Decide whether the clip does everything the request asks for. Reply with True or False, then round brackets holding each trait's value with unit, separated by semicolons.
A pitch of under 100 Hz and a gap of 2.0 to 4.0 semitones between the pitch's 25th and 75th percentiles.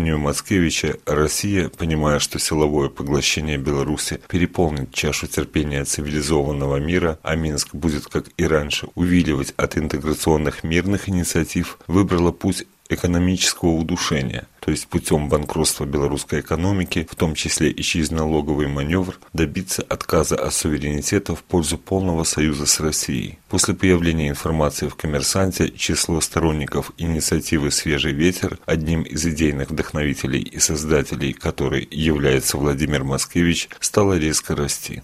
True (80 Hz; 2.8 semitones)